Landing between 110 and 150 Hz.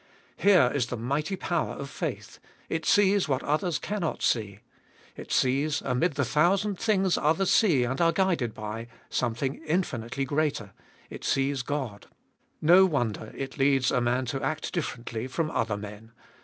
Yes: medium, 140 Hz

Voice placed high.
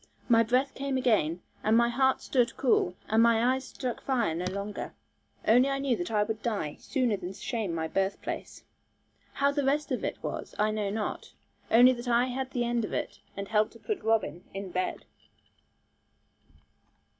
Yes: high, 230 Hz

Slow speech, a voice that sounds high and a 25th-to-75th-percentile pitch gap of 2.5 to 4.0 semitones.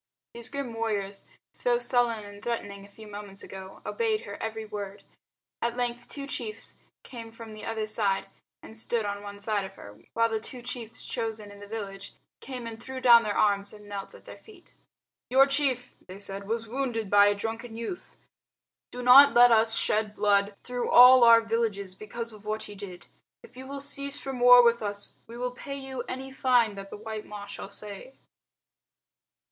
No: average, 195 wpm; high, 225 Hz; average, 3.2 semitones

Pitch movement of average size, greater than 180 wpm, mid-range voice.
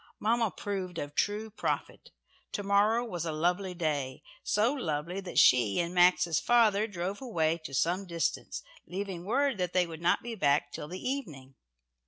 No: average, 4.2 semitones; average, 170 wpm; medium, 180 Hz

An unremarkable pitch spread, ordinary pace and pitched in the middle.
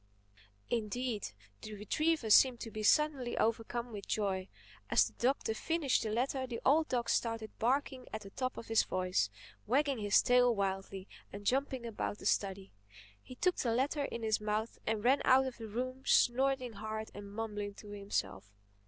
No: average, 3.8 semitones; average, 175 wpm; high, 230 Hz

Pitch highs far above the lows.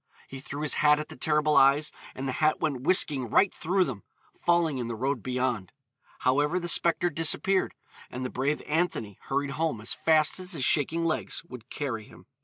No: average, 4.0 semitones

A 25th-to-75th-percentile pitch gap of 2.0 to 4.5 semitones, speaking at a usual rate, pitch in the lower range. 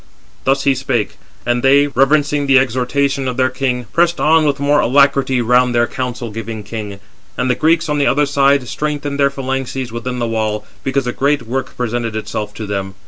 Yes: average, 2.9 semitones; average, 195 wpm; low, 130 Hz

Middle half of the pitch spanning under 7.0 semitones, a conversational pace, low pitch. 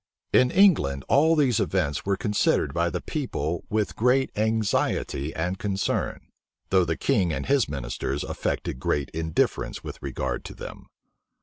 No: wide, 8.1 semitones; average, 145 wpm; very low, 95 Hz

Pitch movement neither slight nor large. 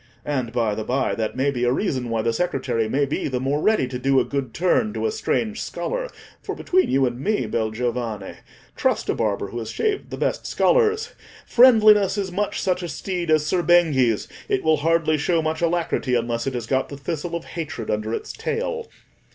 No: wide, 7.2 semitones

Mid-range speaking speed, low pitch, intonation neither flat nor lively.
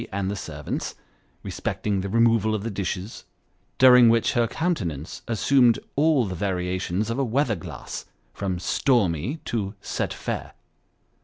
Yes: average, 155 wpm; low, 110 Hz; average, 4.3 semitones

